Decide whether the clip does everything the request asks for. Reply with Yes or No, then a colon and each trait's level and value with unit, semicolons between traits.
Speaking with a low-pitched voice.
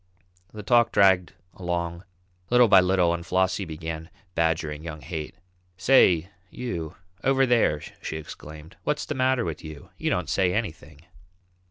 Yes: very low, 90 Hz